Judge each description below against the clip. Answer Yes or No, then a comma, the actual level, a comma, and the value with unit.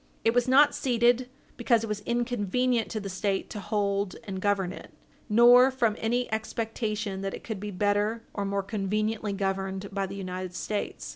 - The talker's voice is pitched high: Yes, high, 210 Hz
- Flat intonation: No, average, 3.1 semitones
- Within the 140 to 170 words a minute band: No, average, 180 wpm